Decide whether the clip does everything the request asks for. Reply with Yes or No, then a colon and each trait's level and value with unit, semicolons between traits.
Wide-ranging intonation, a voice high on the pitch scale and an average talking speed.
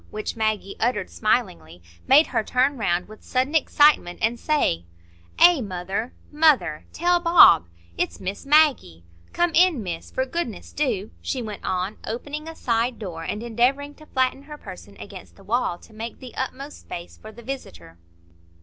Yes: wide, 7.3 semitones; high, 235 Hz; average, 160 wpm